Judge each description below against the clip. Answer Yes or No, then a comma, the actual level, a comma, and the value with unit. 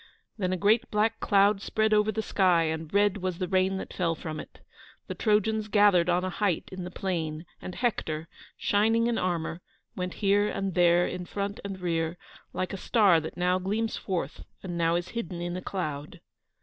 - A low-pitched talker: No, medium, 185 Hz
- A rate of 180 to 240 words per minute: Yes, average, 195 wpm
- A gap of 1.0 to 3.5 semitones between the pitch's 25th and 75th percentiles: Yes, average, 3.0 semitones